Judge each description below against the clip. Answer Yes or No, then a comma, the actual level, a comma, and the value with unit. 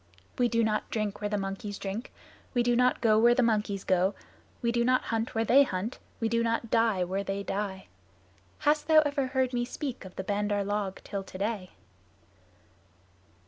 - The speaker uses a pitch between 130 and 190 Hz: No, high, 220 Hz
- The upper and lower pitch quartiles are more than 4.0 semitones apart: No, average, 3.4 semitones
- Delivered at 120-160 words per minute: No, average, 185 wpm